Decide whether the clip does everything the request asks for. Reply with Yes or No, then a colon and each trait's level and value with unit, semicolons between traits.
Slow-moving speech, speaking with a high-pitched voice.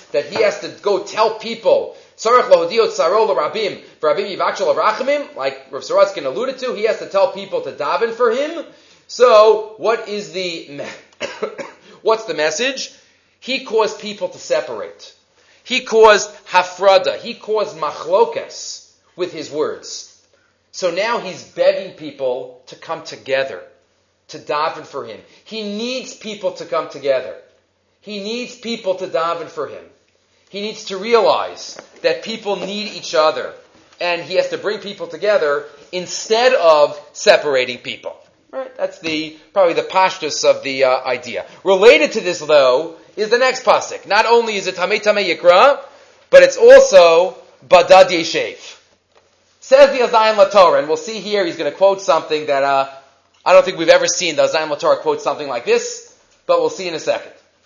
No: average, 160 wpm; high, 225 Hz